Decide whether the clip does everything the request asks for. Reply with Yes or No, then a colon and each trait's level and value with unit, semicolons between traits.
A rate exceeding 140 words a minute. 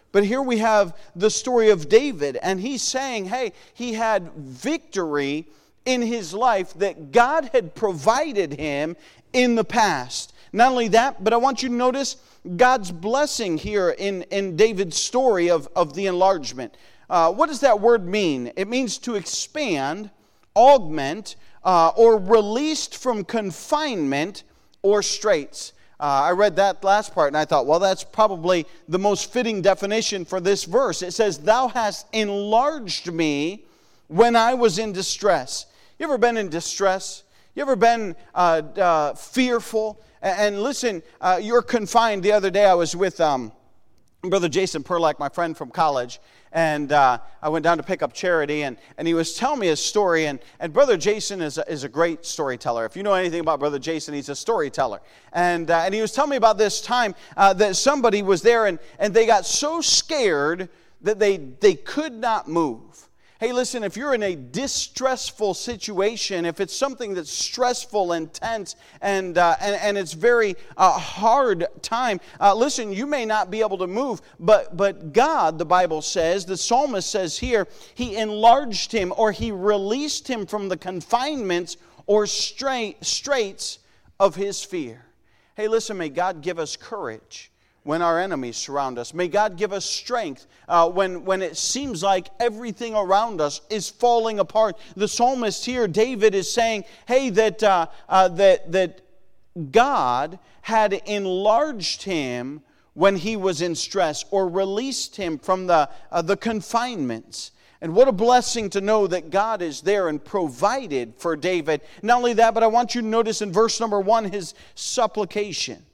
Yes: average, 175 wpm